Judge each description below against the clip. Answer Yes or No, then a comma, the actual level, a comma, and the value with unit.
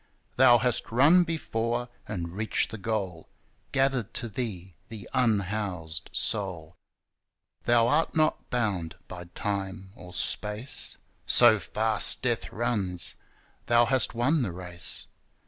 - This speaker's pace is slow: Yes, slow, 120 wpm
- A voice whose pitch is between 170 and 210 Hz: No, low, 110 Hz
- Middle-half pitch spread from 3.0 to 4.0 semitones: No, average, 4.8 semitones